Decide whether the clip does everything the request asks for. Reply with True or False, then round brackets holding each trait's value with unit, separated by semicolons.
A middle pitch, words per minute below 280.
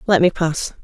True (170 Hz; 215 wpm)